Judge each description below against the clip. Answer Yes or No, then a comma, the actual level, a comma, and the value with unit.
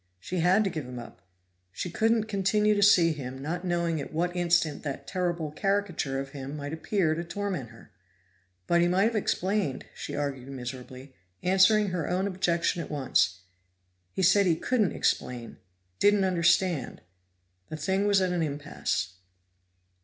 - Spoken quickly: No, average, 160 wpm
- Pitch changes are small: No, average, 5.1 semitones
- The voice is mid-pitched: Yes, medium, 170 Hz